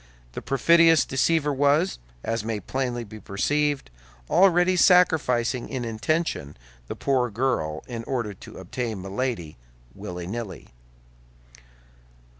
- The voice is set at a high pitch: No, low, 125 Hz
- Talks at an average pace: No, slow, 110 wpm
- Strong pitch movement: Yes, wide, 5.8 semitones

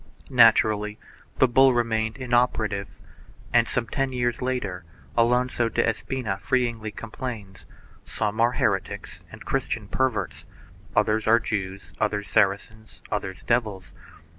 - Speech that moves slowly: Yes, slow, 115 wpm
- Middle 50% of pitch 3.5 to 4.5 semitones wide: No, average, 3.0 semitones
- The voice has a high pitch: No, low, 110 Hz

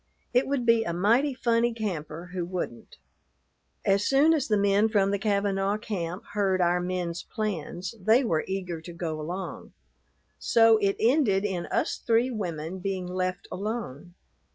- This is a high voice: Yes, high, 195 Hz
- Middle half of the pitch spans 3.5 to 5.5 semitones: Yes, average, 3.9 semitones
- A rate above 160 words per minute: No, average, 155 wpm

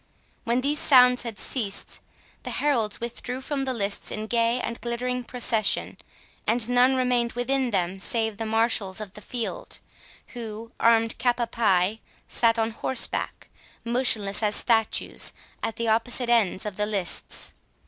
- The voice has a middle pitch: No, high, 230 Hz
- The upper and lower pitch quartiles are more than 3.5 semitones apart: No, narrow, 2.4 semitones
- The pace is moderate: Yes, average, 150 wpm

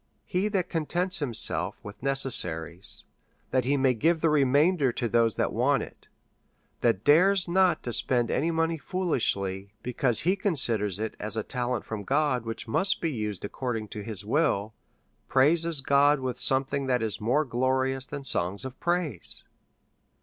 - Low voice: Yes, low, 130 Hz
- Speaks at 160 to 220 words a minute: Yes, average, 165 wpm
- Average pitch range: No, wide, 5.9 semitones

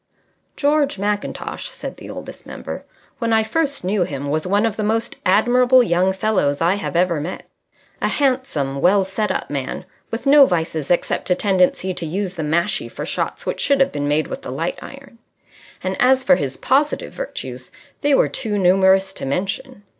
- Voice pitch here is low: No, high, 195 Hz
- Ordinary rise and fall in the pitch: No, wide, 6.4 semitones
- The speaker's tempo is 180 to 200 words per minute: Yes, average, 185 wpm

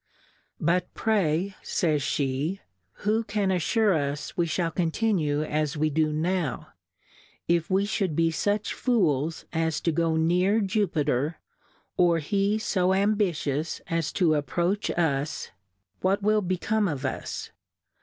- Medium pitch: Yes, medium, 170 Hz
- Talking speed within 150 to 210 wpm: No, slow, 135 wpm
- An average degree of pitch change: Yes, average, 4.4 semitones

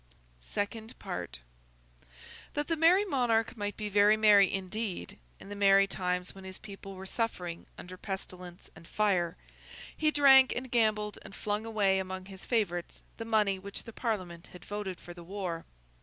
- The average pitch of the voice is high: Yes, high, 200 Hz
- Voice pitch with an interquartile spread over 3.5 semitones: No, average, 3.1 semitones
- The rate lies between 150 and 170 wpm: Yes, average, 165 wpm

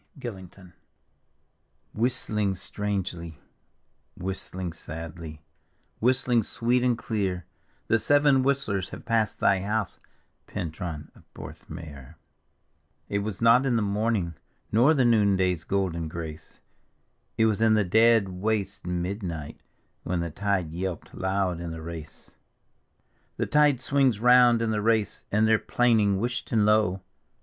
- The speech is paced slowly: Yes, slow, 125 wpm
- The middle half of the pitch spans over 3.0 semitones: Yes, average, 4.4 semitones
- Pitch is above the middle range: No, low, 100 Hz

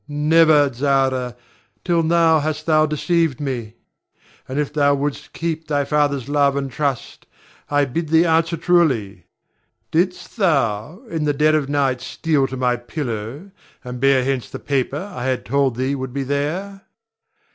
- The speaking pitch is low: No, medium, 145 Hz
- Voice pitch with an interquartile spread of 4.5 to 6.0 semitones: No, average, 3.4 semitones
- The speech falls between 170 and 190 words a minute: No, average, 155 wpm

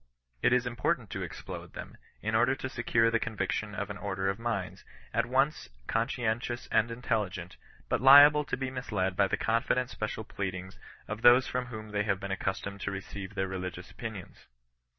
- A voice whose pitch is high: No, low, 110 Hz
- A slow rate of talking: No, average, 180 wpm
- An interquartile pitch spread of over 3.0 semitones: Yes, average, 3.8 semitones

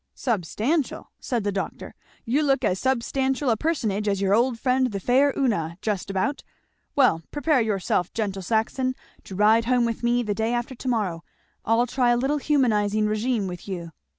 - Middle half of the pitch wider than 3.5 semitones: Yes, average, 4.2 semitones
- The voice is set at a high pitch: Yes, high, 230 Hz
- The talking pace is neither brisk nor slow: Yes, average, 180 wpm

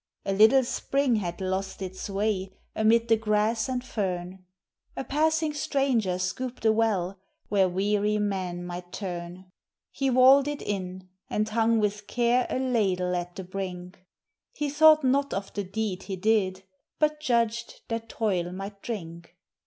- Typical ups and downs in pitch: Yes, average, 4.3 semitones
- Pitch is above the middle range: Yes, high, 210 Hz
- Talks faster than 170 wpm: No, average, 155 wpm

